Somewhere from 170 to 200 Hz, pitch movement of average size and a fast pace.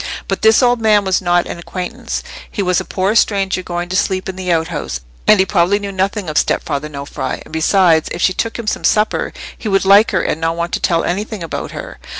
Yes: medium, 185 Hz; average, 3.1 semitones; fast, 230 wpm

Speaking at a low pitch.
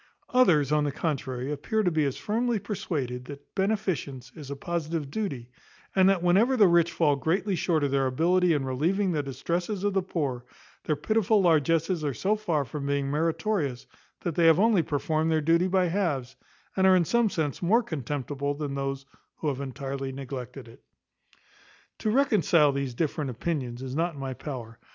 No: medium, 155 Hz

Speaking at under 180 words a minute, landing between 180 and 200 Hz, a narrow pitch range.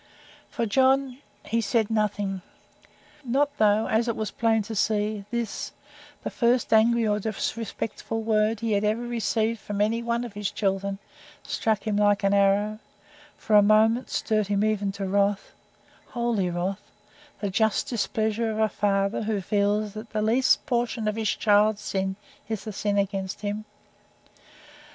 No: average, 155 wpm; high, 215 Hz; narrow, 2.0 semitones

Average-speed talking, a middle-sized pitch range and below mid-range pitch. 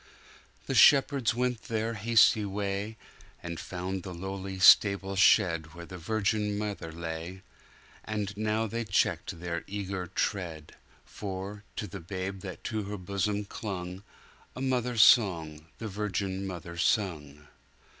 No: slow, 115 wpm; average, 3.0 semitones; low, 100 Hz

